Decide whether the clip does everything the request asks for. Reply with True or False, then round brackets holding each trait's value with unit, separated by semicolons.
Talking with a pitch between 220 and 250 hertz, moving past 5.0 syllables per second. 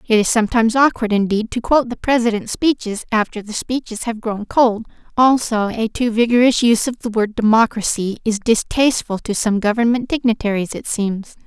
True (225 Hz; 5.5 syllables/s)